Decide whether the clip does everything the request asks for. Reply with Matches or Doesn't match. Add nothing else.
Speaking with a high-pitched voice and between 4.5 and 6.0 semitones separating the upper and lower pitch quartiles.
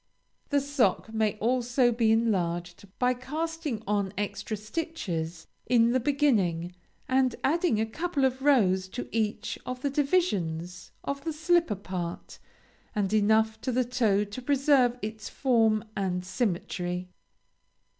Matches